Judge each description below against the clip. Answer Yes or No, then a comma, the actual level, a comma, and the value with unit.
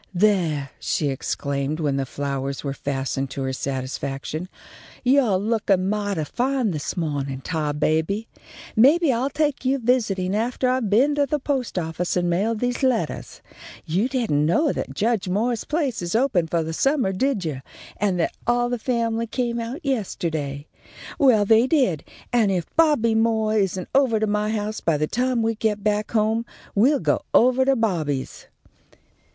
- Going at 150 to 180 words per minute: Yes, average, 165 wpm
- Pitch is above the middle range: Yes, high, 210 Hz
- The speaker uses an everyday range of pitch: No, wide, 7.3 semitones